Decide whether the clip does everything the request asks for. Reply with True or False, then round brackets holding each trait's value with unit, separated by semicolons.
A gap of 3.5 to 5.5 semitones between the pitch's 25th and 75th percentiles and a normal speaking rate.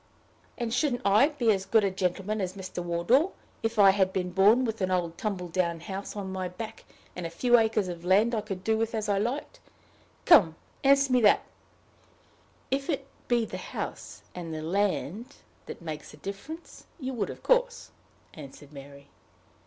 True (4.7 semitones; 185 wpm)